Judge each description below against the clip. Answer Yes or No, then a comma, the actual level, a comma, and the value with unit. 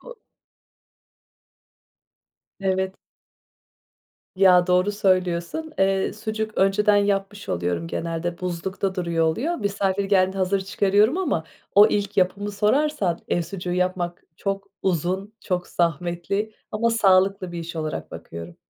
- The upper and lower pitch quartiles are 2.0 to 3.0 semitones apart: Yes, average, 2.7 semitones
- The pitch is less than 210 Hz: Yes, high, 190 Hz